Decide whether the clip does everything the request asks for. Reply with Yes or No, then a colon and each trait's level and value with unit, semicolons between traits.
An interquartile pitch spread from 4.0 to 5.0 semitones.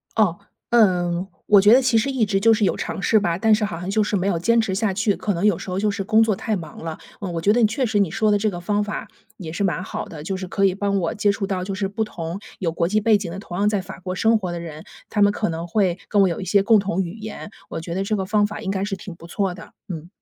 No: average, 3.0 semitones